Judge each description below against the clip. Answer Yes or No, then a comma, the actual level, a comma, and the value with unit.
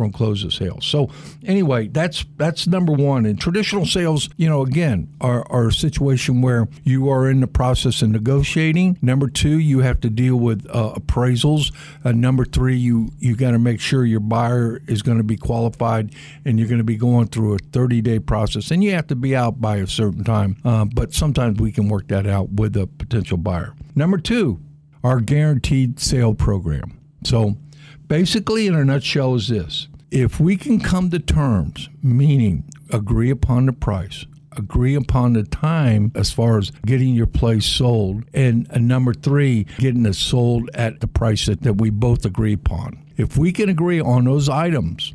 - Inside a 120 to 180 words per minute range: No, average, 195 wpm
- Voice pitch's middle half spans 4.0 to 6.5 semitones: Yes, average, 4.7 semitones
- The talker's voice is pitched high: No, low, 125 Hz